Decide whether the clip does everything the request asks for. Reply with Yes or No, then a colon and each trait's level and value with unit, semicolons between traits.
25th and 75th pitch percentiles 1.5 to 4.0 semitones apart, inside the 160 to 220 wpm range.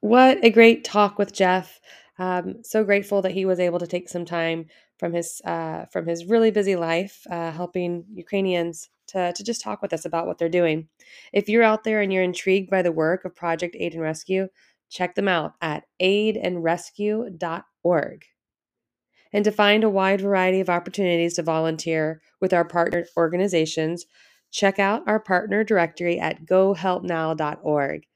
Yes: average, 2.9 semitones; average, 170 wpm